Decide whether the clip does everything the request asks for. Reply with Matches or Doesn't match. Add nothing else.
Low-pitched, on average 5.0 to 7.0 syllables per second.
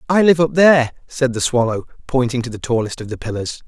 Matches